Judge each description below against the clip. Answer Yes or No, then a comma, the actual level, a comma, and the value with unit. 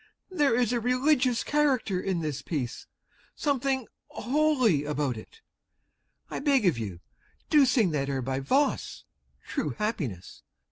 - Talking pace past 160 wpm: No, slow, 135 wpm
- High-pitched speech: Yes, high, 230 Hz